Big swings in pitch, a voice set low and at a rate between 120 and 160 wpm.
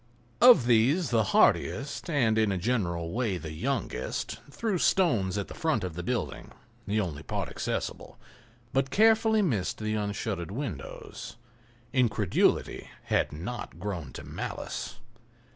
Yes: wide, 6.8 semitones; low, 110 Hz; slow, 135 wpm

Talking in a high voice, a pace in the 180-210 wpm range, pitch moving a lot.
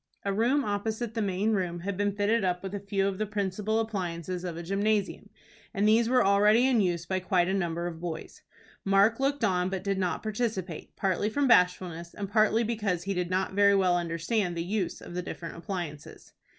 No: high, 195 Hz; fast, 205 wpm; average, 3.1 semitones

